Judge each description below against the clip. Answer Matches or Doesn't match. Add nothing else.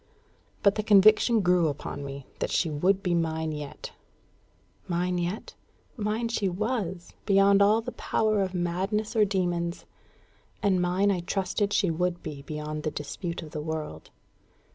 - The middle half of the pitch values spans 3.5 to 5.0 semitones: Matches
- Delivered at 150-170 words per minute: Matches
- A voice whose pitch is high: Doesn't match